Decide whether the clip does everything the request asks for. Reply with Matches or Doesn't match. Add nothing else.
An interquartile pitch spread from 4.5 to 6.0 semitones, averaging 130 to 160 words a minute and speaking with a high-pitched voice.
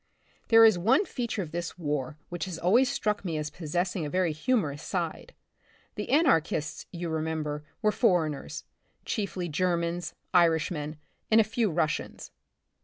Doesn't match